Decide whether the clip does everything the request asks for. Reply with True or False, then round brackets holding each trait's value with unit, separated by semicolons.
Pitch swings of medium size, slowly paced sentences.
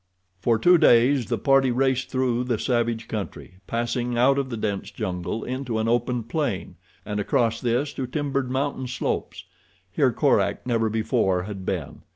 False (3.1 semitones; 165 wpm)